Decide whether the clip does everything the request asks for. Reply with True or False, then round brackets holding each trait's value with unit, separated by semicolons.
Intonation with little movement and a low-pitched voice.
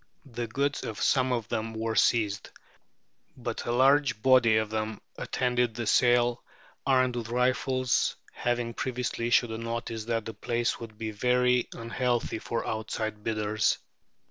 True (2.0 semitones; 120 Hz)